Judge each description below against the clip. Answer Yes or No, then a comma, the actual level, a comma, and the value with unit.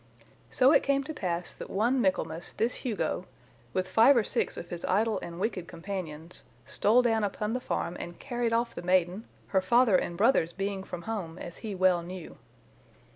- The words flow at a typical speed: Yes, average, 185 wpm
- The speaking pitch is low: No, high, 195 Hz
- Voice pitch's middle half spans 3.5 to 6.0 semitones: Yes, average, 4.7 semitones